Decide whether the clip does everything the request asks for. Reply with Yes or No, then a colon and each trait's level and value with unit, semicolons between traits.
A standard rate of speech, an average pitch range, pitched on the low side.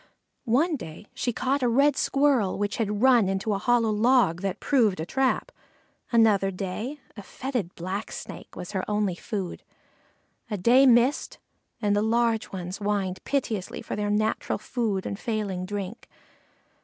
No: average, 155 wpm; average, 3.9 semitones; high, 210 Hz